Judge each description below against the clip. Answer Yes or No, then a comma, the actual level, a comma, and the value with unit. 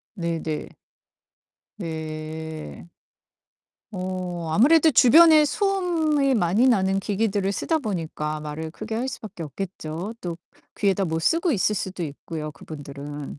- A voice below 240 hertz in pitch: Yes, medium, 185 Hz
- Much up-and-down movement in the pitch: Yes, wide, 6.8 semitones